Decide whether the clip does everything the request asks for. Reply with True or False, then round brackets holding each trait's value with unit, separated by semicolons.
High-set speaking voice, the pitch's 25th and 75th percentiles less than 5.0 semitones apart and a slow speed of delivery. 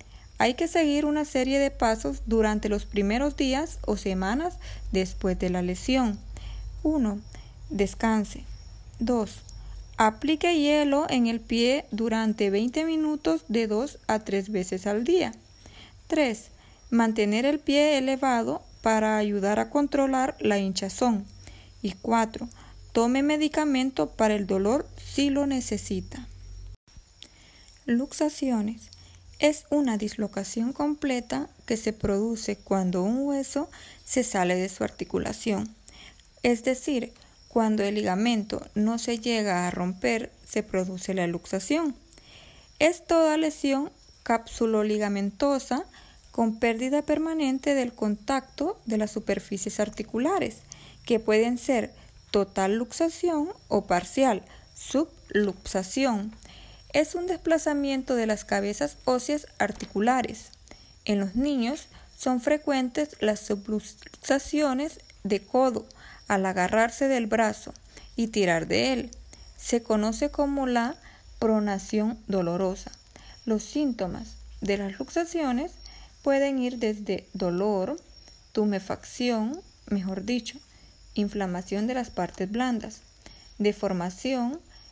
False (230 Hz; 5.4 semitones; 110 wpm)